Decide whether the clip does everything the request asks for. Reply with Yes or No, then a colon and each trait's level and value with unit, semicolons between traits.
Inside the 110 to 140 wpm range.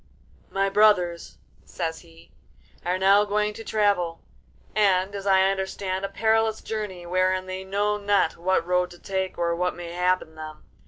No: average, 160 wpm